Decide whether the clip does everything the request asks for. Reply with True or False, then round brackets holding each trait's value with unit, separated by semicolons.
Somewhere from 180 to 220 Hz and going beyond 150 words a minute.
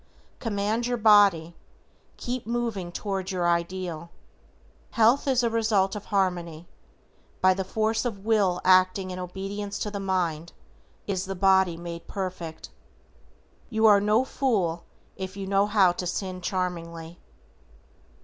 False (190 Hz; 140 wpm)